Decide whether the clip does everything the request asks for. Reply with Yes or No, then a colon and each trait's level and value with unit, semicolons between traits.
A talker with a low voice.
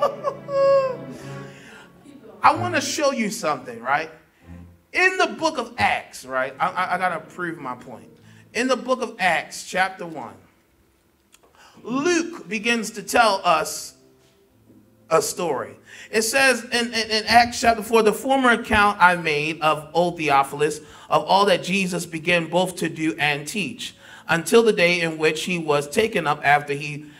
No: medium, 180 Hz